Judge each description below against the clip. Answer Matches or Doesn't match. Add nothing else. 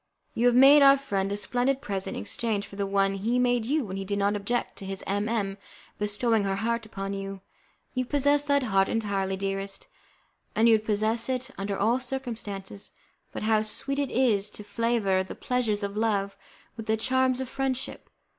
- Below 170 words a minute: Doesn't match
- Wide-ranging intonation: Doesn't match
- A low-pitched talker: Doesn't match